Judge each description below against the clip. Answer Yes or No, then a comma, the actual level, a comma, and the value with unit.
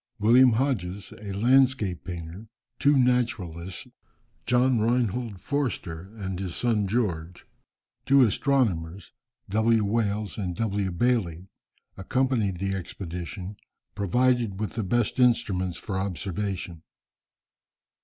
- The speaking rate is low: Yes, slow, 105 wpm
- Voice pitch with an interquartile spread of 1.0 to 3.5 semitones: No, average, 4.7 semitones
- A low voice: Yes, low, 105 Hz